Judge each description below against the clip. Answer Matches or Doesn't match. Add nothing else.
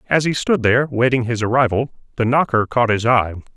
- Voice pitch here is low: Matches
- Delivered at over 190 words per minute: Matches